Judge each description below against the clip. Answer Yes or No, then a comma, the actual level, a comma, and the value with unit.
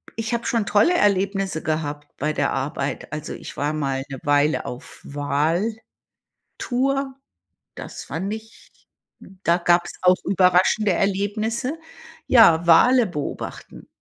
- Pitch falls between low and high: Yes, medium, 180 Hz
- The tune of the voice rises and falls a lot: Yes, wide, 6.0 semitones